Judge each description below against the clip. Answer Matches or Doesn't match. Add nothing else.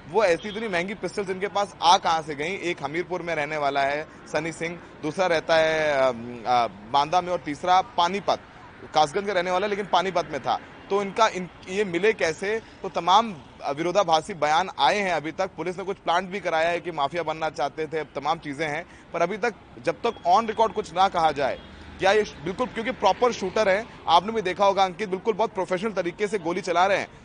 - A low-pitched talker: Doesn't match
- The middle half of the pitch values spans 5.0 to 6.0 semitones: Doesn't match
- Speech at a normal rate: Doesn't match